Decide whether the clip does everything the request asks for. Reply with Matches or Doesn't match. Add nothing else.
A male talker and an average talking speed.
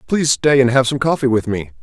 Doesn't match